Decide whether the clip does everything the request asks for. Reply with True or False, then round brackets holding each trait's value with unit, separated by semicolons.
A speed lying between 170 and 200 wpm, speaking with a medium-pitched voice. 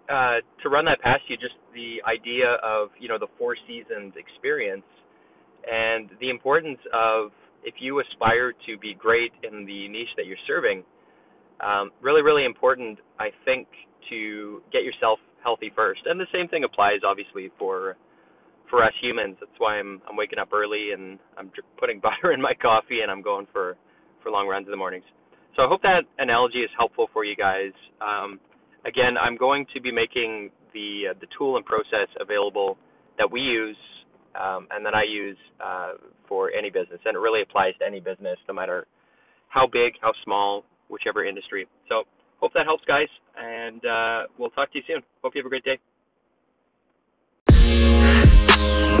False (180 wpm; 130 Hz)